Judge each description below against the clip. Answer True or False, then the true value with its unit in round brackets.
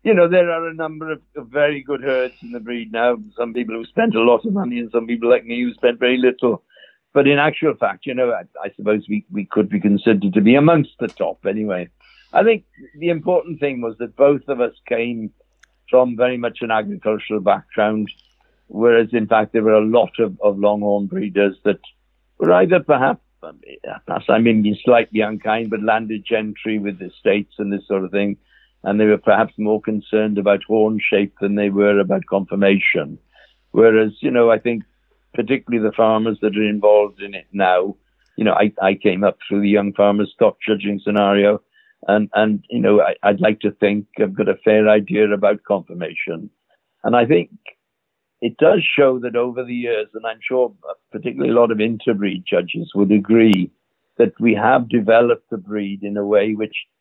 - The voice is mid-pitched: False (110 Hz)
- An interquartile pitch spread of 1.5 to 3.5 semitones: True (2.9 semitones)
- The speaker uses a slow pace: False (195 wpm)